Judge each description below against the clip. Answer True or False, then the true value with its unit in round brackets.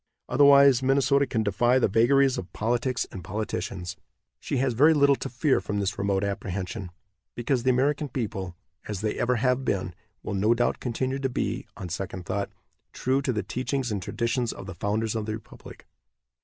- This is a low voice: True (115 Hz)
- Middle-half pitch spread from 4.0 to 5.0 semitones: True (4.7 semitones)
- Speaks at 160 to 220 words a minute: True (185 wpm)